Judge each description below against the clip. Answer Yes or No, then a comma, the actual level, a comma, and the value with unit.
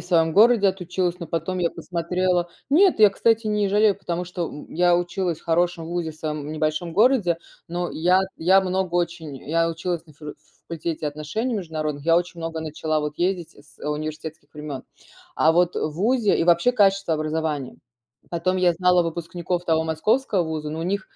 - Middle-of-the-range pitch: Yes, medium, 170 Hz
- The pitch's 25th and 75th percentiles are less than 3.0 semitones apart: Yes, narrow, 2.6 semitones